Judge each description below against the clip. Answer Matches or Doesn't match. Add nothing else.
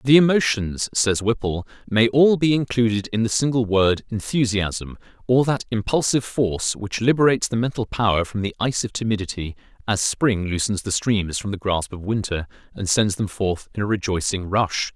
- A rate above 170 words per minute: Matches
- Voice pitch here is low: Matches